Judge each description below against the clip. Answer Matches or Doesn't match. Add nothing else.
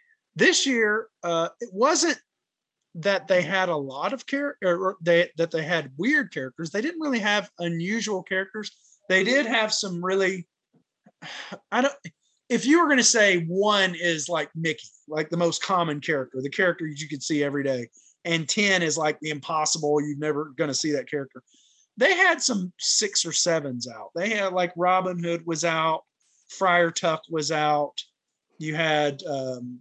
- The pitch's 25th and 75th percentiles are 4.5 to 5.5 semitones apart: Matches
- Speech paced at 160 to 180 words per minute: Matches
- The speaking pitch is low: Doesn't match